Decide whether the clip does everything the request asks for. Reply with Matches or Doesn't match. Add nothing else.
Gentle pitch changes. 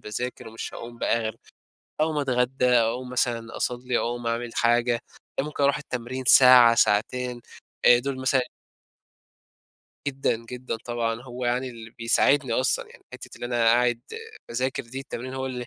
Matches